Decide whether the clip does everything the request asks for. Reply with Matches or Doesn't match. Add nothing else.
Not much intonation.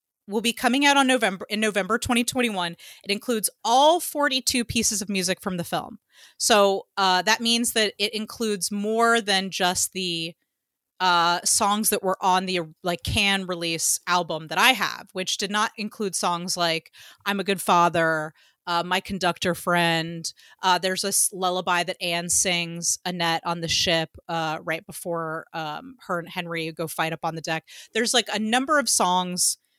Doesn't match